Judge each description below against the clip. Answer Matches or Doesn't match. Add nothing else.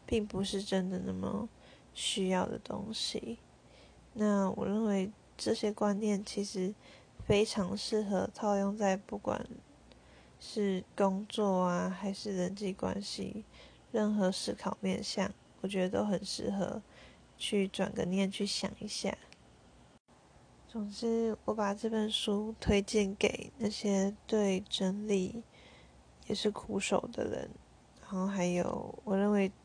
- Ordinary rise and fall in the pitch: Doesn't match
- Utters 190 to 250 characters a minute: Doesn't match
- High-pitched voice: Matches